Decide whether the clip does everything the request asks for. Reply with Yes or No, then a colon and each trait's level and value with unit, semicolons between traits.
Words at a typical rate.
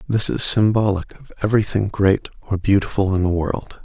Yes: average, 170 wpm